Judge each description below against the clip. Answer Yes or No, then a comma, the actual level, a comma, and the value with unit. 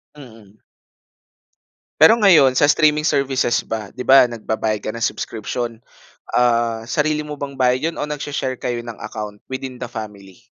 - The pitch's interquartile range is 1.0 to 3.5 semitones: No, average, 4.4 semitones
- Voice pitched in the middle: No, low, 125 Hz